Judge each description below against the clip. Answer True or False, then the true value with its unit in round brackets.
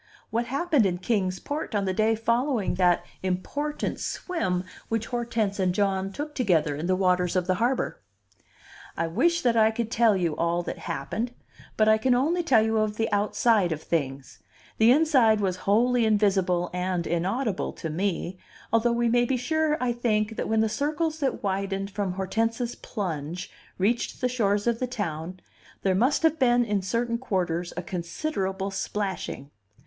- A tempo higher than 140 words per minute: True (175 wpm)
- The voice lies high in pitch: True (210 Hz)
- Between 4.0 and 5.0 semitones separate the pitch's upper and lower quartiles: True (4.7 semitones)